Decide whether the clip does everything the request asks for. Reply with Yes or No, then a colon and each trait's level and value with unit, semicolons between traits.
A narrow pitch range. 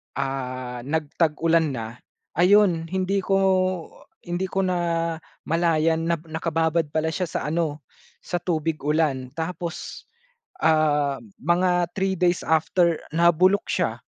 Yes: narrow, 2.2 semitones